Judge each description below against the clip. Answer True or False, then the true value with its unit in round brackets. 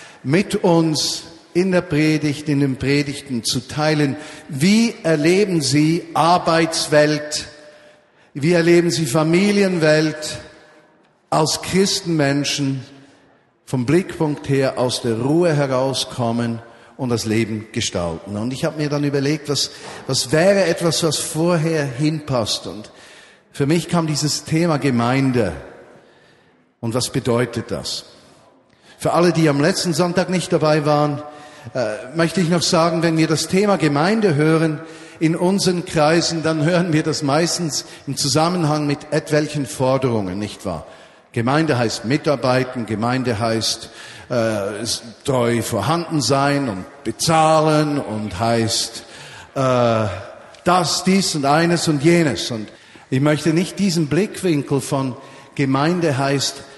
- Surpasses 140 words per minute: False (125 wpm)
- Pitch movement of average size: True (4.0 semitones)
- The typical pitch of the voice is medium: True (150 Hz)